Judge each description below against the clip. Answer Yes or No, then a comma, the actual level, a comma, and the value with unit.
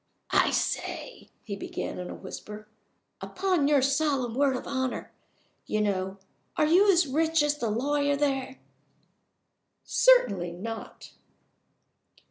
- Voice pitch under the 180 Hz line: No, very high, 270 Hz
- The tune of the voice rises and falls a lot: Yes, wide, 5.8 semitones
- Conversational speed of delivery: No, slow, 120 wpm